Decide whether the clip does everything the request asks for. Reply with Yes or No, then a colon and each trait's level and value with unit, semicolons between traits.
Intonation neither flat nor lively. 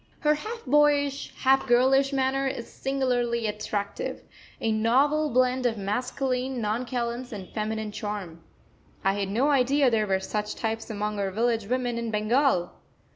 Yes: average, 4.0 semitones